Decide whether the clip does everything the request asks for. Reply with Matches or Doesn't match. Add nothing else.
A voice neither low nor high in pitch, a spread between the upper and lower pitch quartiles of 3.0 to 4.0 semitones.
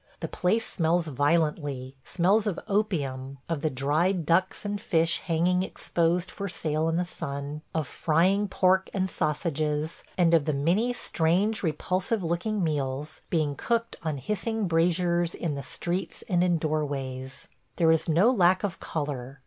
Matches